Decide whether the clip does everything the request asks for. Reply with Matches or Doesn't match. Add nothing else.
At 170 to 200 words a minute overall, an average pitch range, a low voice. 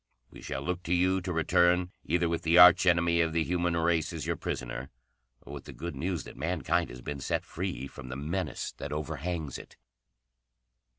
Matches